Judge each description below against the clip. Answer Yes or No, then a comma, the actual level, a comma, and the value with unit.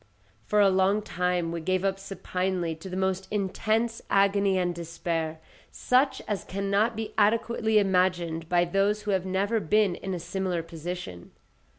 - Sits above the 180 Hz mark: Yes, high, 190 Hz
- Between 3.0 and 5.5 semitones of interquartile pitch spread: No, narrow, 2.6 semitones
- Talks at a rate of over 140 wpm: Yes, average, 160 wpm